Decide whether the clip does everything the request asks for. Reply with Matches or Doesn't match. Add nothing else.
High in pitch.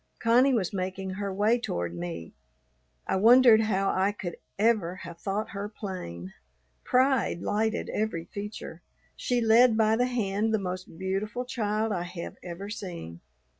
Matches